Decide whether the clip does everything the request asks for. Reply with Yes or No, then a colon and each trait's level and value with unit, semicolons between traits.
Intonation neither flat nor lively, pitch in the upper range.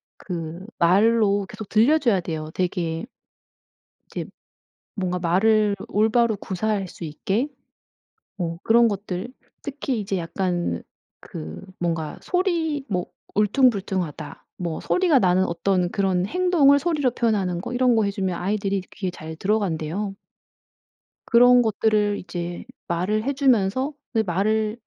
Yes: average, 4.6 semitones; high, 200 Hz